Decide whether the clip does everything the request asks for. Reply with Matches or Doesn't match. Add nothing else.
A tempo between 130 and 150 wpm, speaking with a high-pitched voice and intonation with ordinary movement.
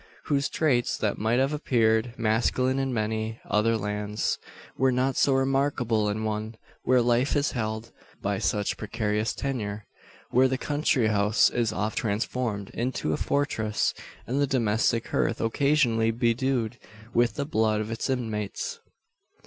Doesn't match